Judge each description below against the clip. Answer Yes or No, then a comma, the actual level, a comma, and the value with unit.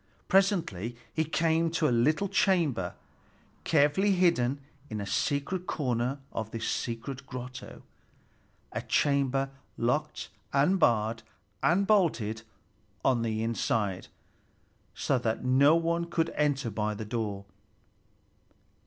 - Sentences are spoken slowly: Yes, slow, 115 wpm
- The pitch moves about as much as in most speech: No, wide, 6.3 semitones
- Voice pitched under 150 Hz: Yes, low, 135 Hz